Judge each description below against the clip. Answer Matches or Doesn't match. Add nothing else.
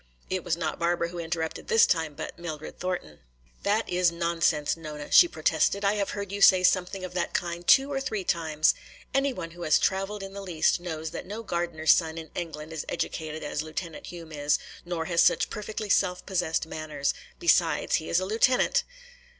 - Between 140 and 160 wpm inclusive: Doesn't match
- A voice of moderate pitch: Matches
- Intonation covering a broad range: Doesn't match